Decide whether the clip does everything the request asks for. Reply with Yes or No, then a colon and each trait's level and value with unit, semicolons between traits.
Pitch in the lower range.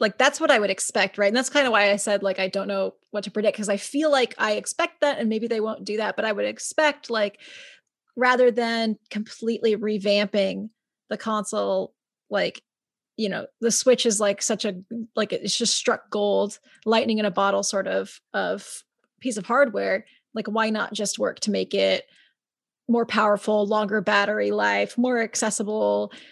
No: high, 215 Hz